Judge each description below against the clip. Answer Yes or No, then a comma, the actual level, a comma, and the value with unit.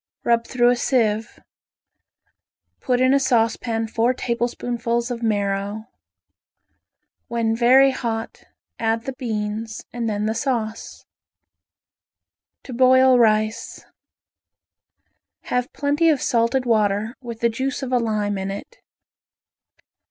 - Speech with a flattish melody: Yes, narrow, 2.3 semitones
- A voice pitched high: Yes, high, 235 Hz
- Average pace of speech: No, slow, 115 wpm